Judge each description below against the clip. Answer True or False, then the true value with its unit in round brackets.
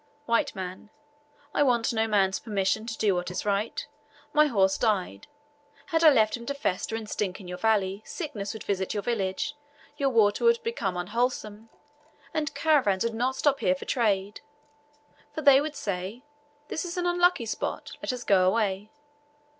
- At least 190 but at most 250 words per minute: False (175 wpm)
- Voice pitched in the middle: False (220 Hz)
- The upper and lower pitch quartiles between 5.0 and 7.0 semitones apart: True (5.5 semitones)